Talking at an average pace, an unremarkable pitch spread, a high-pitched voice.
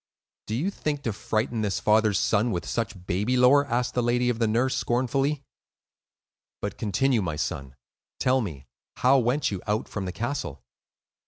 No: average, 170 wpm; average, 3.8 semitones; low, 115 Hz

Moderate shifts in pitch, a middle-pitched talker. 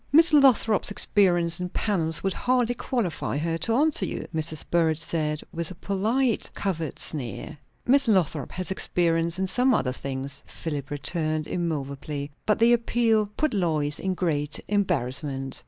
No: wide, 5.9 semitones; medium, 170 Hz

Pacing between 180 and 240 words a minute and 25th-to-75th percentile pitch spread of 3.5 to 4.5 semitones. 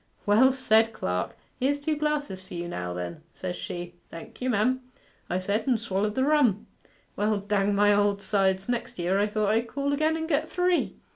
No: average, 195 wpm; wide, 5.6 semitones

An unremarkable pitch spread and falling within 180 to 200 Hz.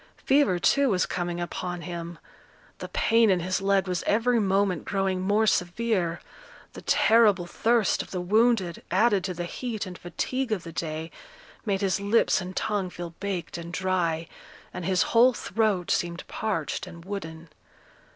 Yes: average, 3.6 semitones; medium, 185 Hz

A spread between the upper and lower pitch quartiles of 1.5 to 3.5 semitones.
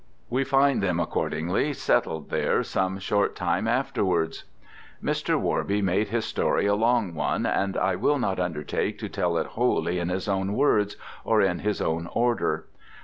No: average, 4.1 semitones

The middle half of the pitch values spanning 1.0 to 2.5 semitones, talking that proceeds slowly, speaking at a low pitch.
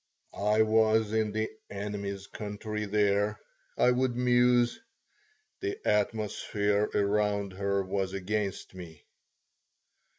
Yes: narrow, 1.7 semitones; slow, 100 wpm; low, 105 Hz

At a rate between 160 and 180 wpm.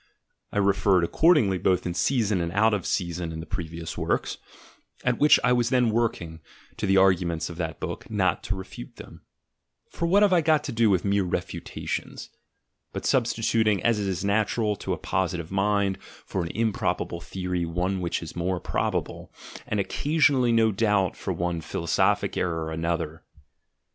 Yes: average, 175 wpm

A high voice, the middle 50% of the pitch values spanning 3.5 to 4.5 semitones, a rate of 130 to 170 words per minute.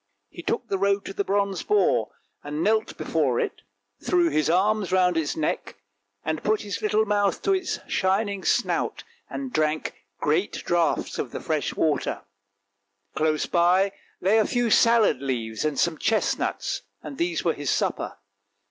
No: high, 195 Hz; wide, 5.4 semitones; average, 155 wpm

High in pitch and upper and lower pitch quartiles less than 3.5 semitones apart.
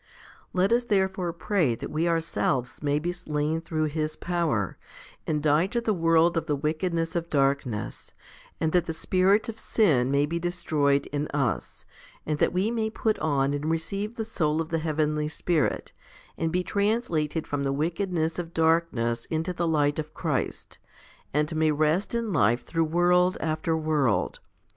No: medium, 160 Hz; average, 3.1 semitones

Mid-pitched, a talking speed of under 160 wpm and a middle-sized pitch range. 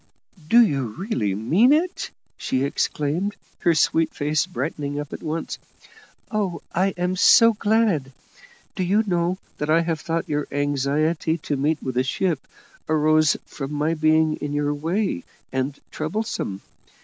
Yes: medium, 155 Hz; average, 145 wpm; average, 3.9 semitones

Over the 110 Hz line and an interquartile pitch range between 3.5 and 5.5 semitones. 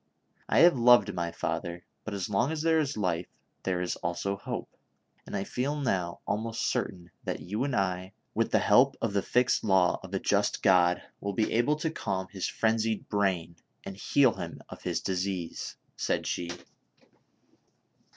No: low, 100 Hz; average, 4.6 semitones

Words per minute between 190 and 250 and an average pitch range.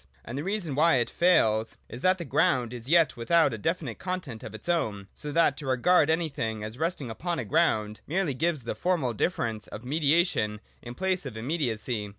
No: average, 200 wpm; wide, 7.0 semitones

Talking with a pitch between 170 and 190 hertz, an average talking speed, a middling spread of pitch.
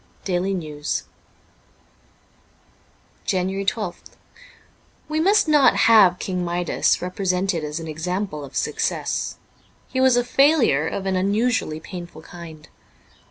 No: medium, 185 Hz; slow, 120 wpm; average, 4.5 semitones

